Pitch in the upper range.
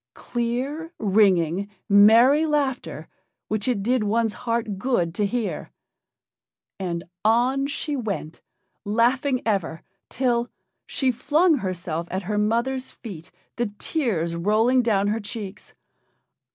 Yes: high, 225 Hz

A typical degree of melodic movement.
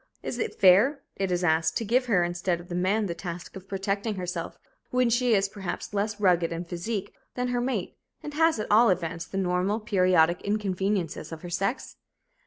Yes: average, 3.6 semitones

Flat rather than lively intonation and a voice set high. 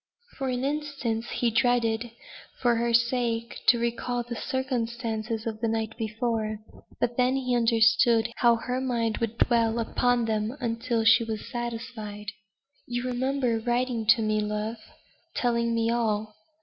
Yes: narrow, 1.5 semitones; high, 235 Hz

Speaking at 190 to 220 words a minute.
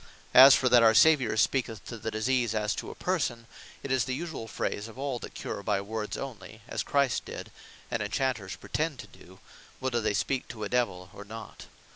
Yes: fast, 205 wpm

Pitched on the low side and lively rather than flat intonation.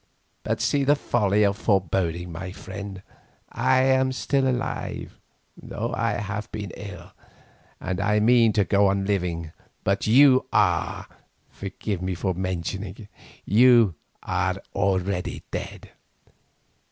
No: low, 100 Hz; average, 3.5 semitones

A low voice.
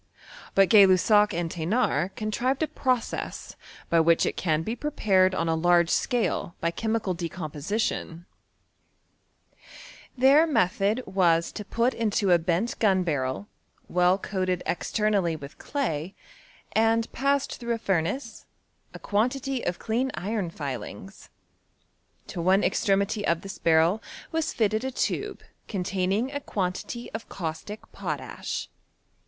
No: high, 195 Hz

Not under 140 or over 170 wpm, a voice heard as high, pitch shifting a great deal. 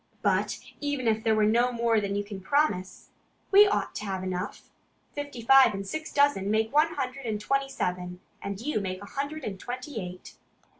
No: average, 195 wpm; high, 225 Hz; wide, 5.8 semitones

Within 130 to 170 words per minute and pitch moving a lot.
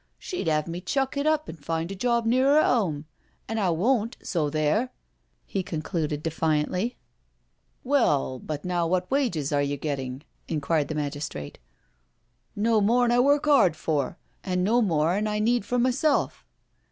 No: average, 190 wpm; wide, 7.8 semitones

